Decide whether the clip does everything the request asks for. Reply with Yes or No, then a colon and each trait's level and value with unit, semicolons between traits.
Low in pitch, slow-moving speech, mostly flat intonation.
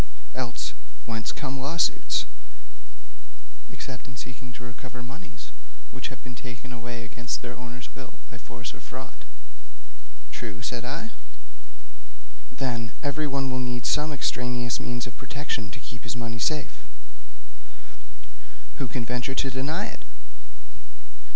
Yes: low, 125 Hz; slow, 130 wpm; narrow, 1.9 semitones